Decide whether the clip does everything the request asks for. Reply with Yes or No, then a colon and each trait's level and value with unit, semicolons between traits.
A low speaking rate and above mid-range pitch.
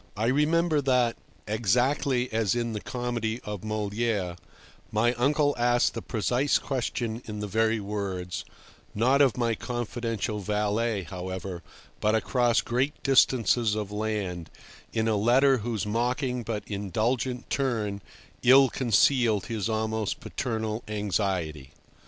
No: slow, 120 wpm; low, 115 Hz